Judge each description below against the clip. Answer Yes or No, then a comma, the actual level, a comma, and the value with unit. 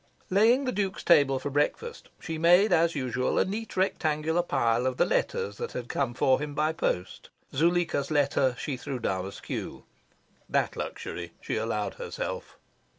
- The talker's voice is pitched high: No, medium, 145 Hz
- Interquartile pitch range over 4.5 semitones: Yes, wide, 5.4 semitones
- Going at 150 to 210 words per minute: Yes, average, 160 wpm